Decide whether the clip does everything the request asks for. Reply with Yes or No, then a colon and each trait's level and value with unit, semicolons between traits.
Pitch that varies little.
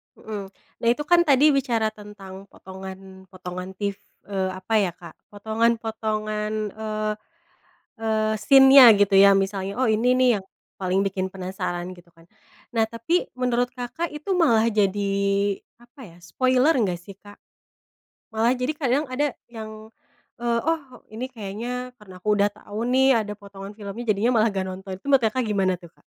No: average, 4.2 semitones